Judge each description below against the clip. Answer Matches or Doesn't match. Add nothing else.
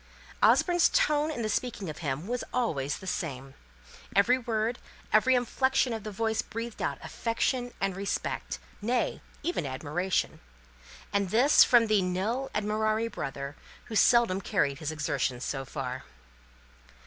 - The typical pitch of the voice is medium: Doesn't match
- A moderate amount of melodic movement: Doesn't match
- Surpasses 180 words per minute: Doesn't match